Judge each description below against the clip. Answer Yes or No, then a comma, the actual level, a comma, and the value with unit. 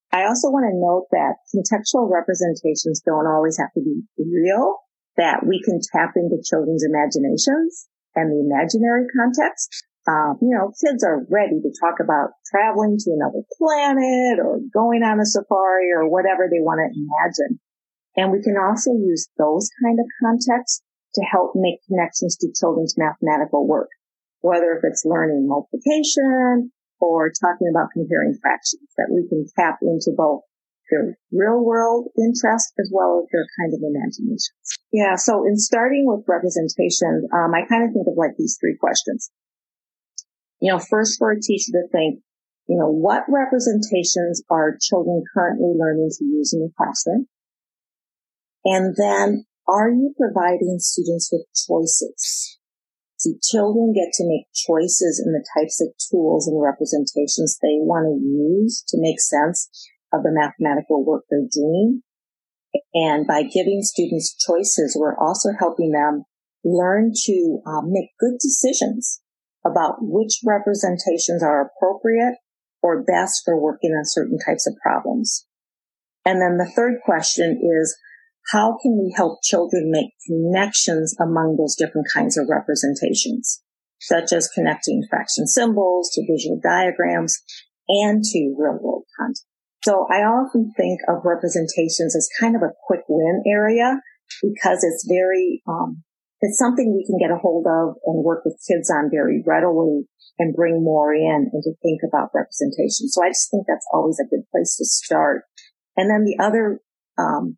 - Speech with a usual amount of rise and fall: No, wide, 5.9 semitones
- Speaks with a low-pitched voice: No, medium, 185 Hz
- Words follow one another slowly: No, average, 155 wpm